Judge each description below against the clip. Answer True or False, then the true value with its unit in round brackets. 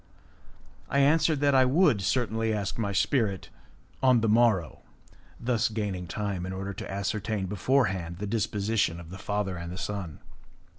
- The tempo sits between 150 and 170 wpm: True (165 wpm)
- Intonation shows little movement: False (3.8 semitones)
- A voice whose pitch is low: True (105 Hz)